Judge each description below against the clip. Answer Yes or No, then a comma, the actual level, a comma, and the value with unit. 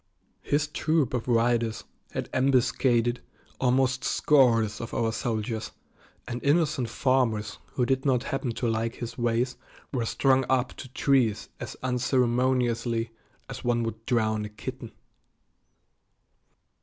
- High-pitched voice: No, low, 120 Hz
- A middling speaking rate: No, slow, 125 wpm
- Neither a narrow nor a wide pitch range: No, narrow, 2.3 semitones